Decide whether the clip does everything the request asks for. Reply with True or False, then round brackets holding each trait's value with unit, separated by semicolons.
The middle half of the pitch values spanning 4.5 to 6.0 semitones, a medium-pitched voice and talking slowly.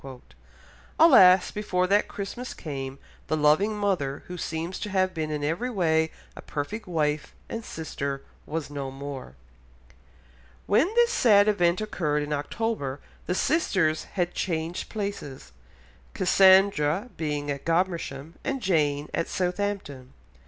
True (5.4 semitones; 170 Hz; 130 wpm)